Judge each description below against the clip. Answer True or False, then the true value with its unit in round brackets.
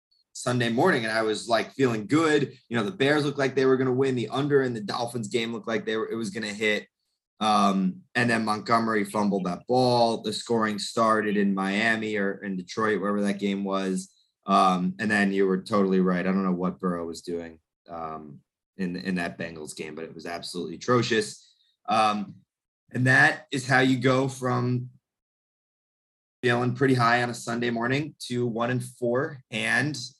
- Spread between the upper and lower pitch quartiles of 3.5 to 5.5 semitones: True (4.4 semitones)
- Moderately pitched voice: False (115 Hz)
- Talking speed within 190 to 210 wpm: True (195 wpm)